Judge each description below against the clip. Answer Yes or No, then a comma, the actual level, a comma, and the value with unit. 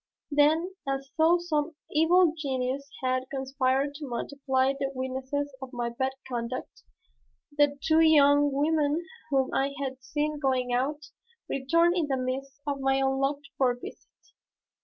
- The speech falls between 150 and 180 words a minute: No, average, 140 wpm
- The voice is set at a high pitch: Yes, very high, 275 Hz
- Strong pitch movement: No, narrow, 2.1 semitones